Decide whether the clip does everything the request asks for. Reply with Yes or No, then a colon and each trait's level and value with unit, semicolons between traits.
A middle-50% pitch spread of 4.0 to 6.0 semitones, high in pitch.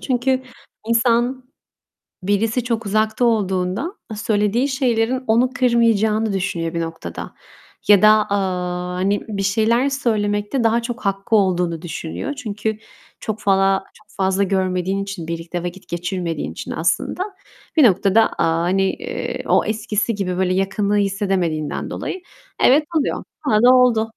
No: average, 3.6 semitones; high, 205 Hz